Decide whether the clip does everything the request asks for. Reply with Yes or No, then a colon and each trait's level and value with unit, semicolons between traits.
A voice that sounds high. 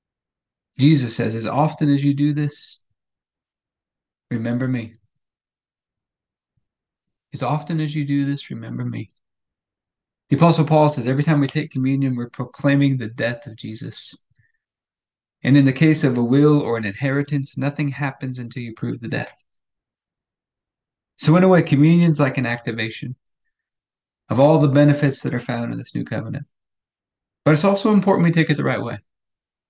No: medium, 140 Hz